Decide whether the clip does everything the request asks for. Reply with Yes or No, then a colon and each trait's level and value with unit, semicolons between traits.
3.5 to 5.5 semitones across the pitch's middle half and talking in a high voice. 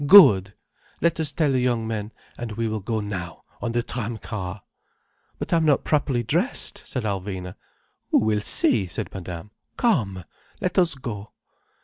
No: average, 4.9 semitones; low, 110 Hz